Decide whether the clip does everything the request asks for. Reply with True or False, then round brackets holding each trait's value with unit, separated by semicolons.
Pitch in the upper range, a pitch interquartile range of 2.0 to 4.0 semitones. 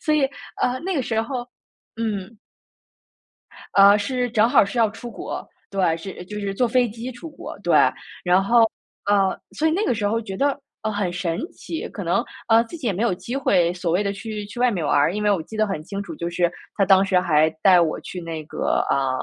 False (205 Hz; 4.6 semitones)